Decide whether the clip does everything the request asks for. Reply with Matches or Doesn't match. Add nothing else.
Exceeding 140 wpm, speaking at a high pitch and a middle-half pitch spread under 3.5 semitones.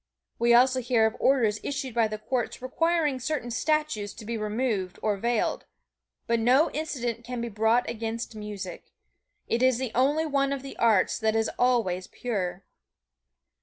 Matches